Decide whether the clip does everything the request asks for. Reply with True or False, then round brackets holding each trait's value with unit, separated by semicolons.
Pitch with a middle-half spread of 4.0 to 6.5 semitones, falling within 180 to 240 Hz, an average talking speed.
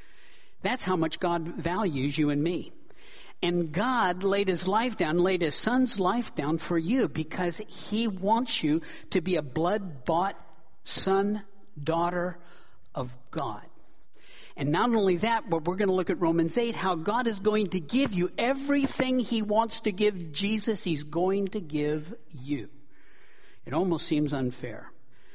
True (5.2 semitones; 185 Hz; 160 wpm)